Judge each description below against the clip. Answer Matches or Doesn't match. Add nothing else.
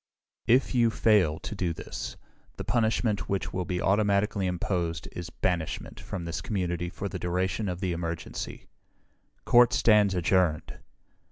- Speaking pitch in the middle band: Doesn't match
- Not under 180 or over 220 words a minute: Doesn't match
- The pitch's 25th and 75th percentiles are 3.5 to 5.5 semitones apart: Doesn't match